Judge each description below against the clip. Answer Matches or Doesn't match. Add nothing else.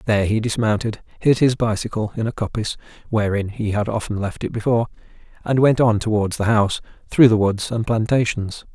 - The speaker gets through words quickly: Doesn't match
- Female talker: Doesn't match